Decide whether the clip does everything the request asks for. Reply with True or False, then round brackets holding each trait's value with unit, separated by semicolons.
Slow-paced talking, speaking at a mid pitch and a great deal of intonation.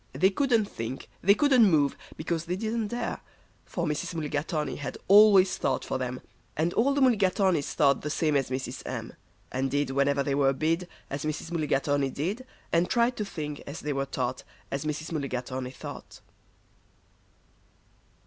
False (165 wpm; 155 Hz; 5.8 semitones)